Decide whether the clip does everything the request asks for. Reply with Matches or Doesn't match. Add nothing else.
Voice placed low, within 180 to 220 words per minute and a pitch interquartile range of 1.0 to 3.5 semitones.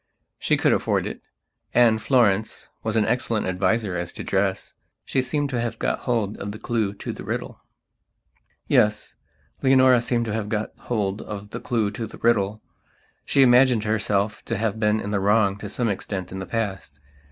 Matches